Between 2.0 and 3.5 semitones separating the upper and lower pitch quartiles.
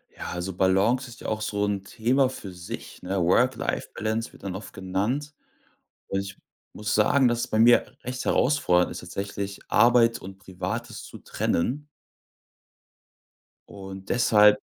No: average, 4.0 semitones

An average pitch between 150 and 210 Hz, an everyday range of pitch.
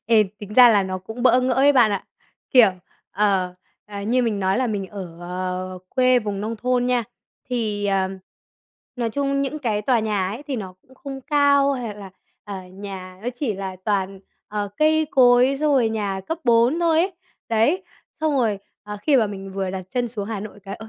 No: high, 220 Hz; average, 4.3 semitones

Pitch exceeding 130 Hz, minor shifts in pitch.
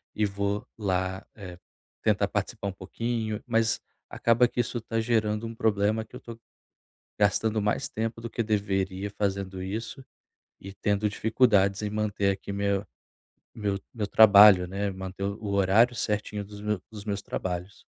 No: low, 105 Hz; narrow, 2.2 semitones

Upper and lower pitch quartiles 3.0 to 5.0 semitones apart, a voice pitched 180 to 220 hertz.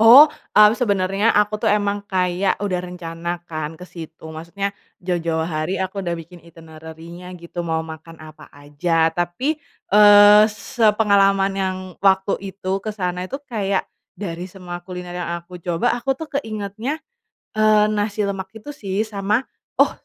Yes: average, 3.3 semitones; high, 190 Hz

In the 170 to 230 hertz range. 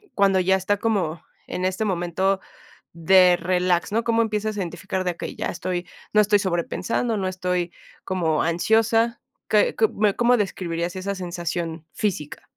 Yes: medium, 185 Hz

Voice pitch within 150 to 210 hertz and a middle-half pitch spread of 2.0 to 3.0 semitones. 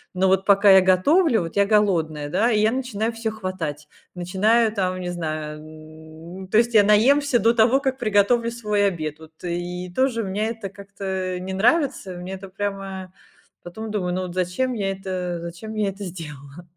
No: high, 190 Hz; average, 3.7 semitones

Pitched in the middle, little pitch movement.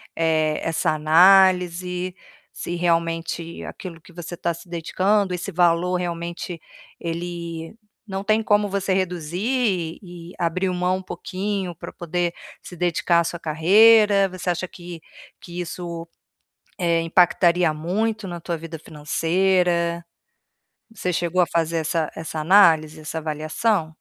Yes: medium, 175 Hz; narrow, 1.9 semitones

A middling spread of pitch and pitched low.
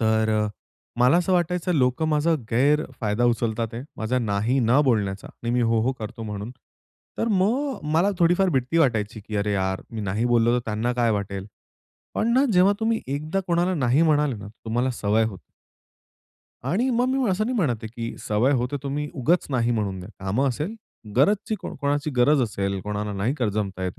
No: wide, 6.7 semitones; low, 125 Hz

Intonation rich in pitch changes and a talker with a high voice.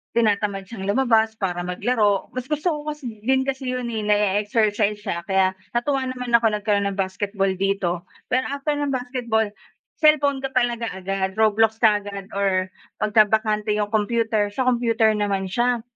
No: average, 3.7 semitones; high, 215 Hz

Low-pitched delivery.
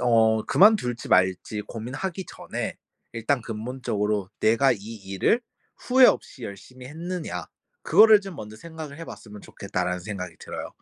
Yes: low, 115 Hz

